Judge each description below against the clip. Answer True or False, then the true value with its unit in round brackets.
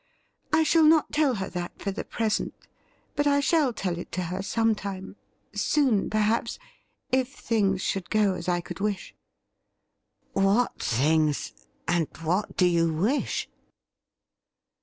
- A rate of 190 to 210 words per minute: False (150 wpm)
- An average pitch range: False (5.7 semitones)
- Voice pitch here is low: False (200 Hz)